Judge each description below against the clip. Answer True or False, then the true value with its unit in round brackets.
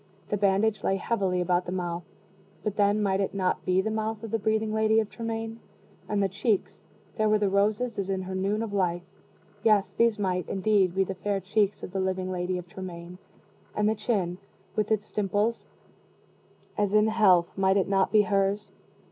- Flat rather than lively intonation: True (2.3 semitones)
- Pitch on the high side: True (200 Hz)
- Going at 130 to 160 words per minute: False (195 wpm)